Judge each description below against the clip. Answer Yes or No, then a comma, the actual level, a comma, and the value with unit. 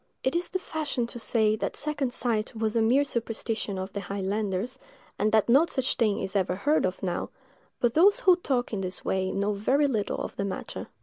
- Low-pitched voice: No, high, 225 Hz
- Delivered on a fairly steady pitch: No, average, 5.0 semitones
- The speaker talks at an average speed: No, fast, 210 wpm